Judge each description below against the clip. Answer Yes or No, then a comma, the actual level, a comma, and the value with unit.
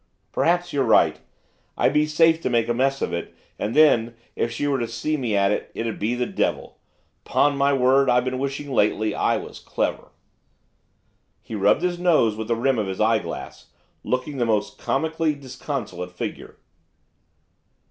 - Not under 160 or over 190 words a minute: Yes, average, 175 wpm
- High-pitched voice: No, low, 125 Hz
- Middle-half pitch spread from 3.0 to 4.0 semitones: No, average, 4.4 semitones